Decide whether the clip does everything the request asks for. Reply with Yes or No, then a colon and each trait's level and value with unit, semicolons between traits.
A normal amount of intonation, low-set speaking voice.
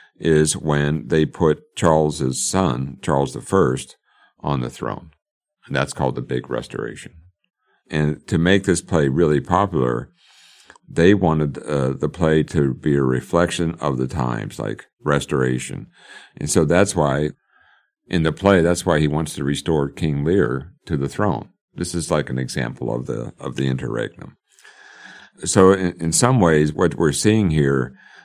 Yes: average, 3.9 semitones; very low, 75 Hz